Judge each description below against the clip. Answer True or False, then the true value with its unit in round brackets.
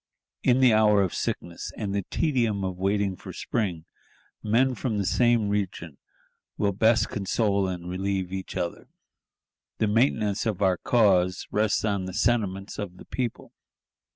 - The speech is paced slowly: False (155 wpm)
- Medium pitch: False (100 Hz)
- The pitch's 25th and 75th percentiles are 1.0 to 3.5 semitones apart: True (2.9 semitones)